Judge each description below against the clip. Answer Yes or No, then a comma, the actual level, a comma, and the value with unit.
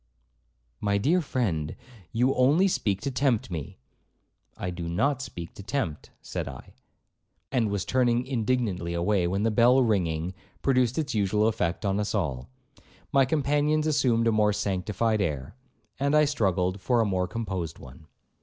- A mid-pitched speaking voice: No, low, 105 Hz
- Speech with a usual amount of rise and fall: No, wide, 6.0 semitones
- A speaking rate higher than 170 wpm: No, average, 155 wpm